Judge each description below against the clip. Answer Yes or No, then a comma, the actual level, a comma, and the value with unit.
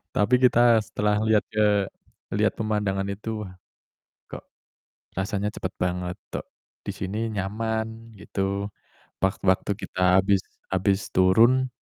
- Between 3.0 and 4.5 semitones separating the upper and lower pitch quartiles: No, narrow, 2.5 semitones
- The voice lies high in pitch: No, low, 105 Hz